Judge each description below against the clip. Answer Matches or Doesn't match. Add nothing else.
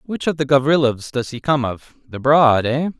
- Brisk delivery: Matches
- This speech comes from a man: Matches